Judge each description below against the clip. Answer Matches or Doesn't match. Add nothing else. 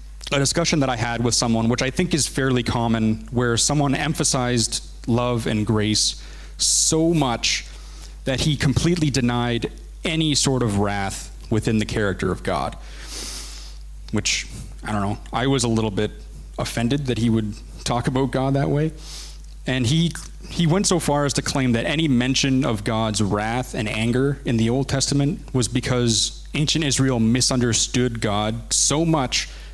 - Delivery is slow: Doesn't match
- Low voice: Matches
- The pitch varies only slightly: Doesn't match